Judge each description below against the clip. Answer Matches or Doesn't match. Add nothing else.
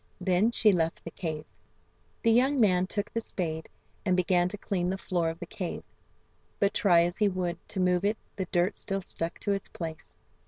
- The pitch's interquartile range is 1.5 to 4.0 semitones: Matches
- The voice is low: Doesn't match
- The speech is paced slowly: Doesn't match